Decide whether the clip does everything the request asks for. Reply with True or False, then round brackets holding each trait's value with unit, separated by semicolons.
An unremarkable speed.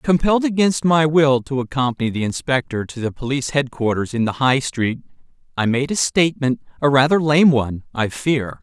True (180 wpm)